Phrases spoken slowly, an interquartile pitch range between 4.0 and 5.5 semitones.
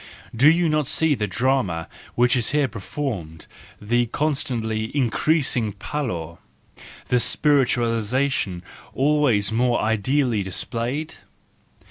Yes: slow, 105 wpm; average, 4.8 semitones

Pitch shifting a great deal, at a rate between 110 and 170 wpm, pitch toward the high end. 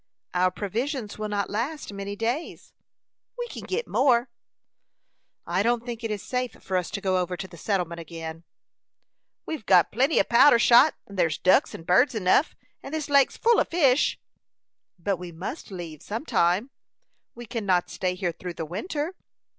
No: wide, 6.0 semitones; average, 180 wpm; high, 205 Hz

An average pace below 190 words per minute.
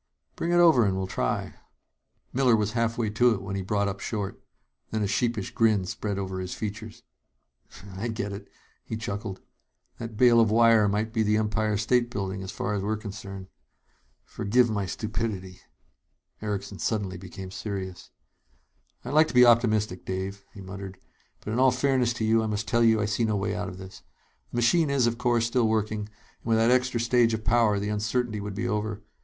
No: average, 195 wpm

